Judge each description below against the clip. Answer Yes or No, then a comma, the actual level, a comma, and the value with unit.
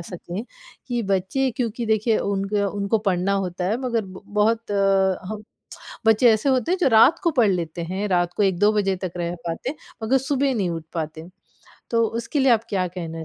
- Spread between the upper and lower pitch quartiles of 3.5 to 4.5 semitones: Yes, average, 4.1 semitones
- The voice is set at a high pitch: Yes, high, 200 Hz